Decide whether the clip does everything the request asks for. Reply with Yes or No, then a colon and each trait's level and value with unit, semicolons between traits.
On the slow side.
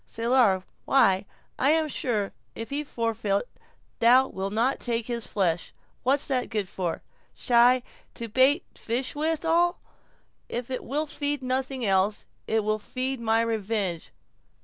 Yes: slow, 130 wpm